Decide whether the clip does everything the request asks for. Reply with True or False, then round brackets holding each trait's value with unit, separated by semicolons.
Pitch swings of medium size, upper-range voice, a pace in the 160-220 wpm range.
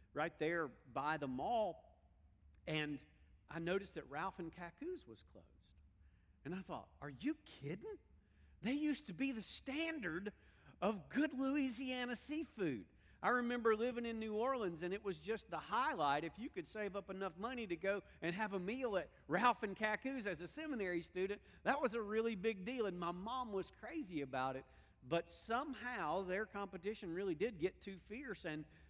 False (6.7 semitones; 200 Hz; 180 wpm)